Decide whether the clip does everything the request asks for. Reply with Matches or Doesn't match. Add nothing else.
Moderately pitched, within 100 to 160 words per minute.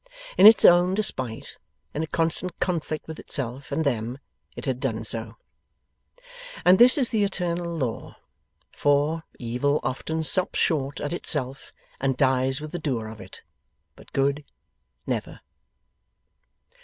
Matches